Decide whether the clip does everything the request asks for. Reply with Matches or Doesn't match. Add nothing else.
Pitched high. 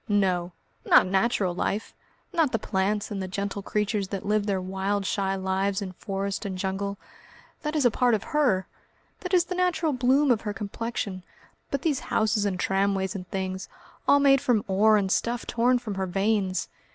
Matches